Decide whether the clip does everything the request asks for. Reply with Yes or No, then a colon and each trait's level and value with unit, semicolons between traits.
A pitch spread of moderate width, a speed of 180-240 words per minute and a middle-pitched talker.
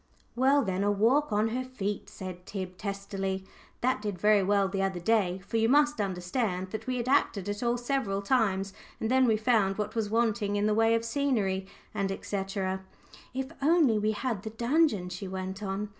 No: average, 3.6 semitones; average, 190 wpm; high, 210 Hz